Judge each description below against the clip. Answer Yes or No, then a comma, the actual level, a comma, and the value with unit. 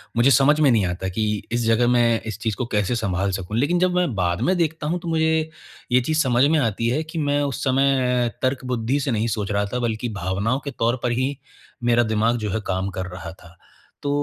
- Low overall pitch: Yes, low, 120 Hz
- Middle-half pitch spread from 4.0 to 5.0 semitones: Yes, average, 4.7 semitones